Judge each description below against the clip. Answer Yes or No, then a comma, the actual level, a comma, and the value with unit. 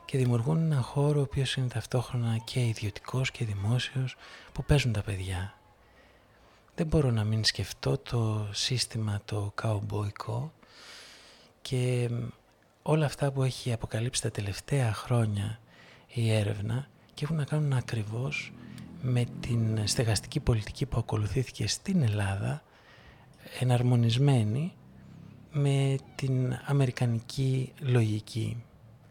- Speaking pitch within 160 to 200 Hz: No, low, 120 Hz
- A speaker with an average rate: No, slow, 110 wpm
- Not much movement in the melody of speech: No, average, 3.4 semitones